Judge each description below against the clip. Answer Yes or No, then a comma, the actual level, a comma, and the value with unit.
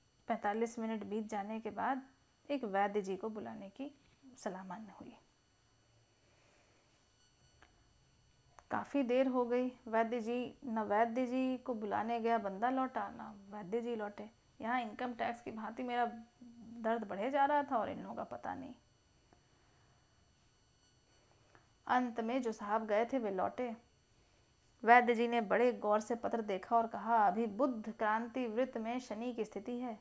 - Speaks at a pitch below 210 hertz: No, high, 230 Hz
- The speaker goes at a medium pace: Yes, average, 155 wpm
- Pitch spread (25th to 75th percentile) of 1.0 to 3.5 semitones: Yes, average, 2.8 semitones